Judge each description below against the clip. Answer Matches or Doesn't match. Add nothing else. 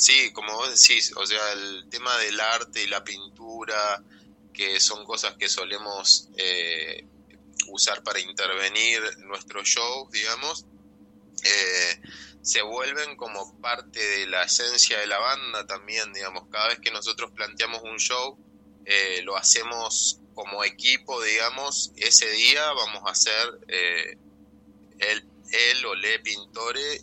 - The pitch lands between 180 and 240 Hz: Doesn't match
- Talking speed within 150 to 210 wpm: Doesn't match